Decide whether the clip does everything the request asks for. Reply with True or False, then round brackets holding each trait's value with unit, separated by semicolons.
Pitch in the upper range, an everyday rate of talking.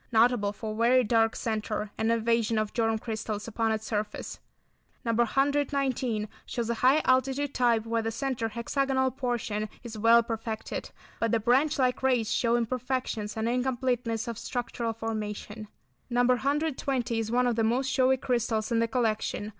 True (235 Hz; 160 wpm)